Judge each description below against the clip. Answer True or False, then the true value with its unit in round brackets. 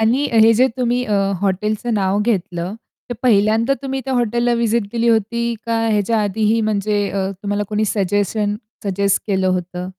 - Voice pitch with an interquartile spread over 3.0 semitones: False (2.7 semitones)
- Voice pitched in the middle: False (215 Hz)